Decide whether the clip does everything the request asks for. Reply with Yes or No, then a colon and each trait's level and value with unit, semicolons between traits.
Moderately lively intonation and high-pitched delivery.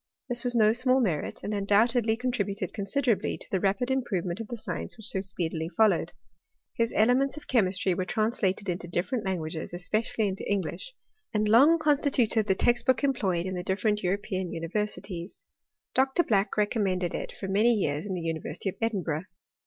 Yes: average, 4.3 semitones; high, 205 Hz